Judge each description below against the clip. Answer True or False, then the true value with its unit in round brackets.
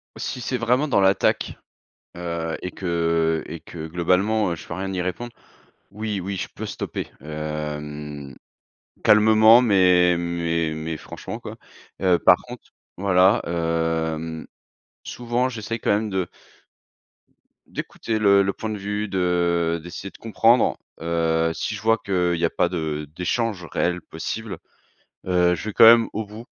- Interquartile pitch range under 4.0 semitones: False (4.3 semitones)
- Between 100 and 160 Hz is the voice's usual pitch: False (90 Hz)